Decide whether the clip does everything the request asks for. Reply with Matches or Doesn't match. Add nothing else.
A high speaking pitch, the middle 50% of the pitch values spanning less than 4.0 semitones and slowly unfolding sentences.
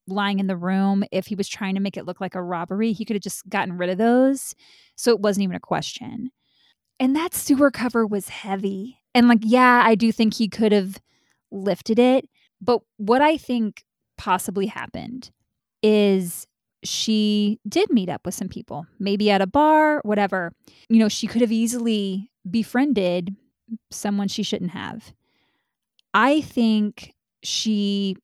Doesn't match